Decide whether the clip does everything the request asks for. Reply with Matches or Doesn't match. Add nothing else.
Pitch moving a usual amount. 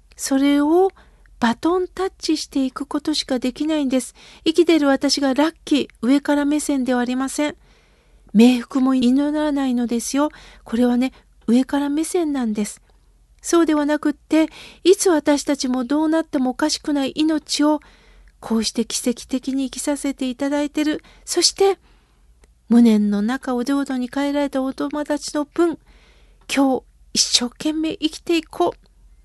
Matches